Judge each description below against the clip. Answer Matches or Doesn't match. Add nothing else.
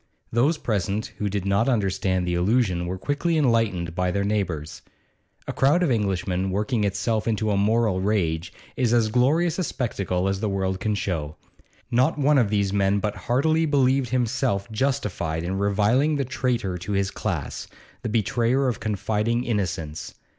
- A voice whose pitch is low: Matches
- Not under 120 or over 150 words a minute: Doesn't match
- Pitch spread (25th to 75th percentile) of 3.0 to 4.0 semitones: Doesn't match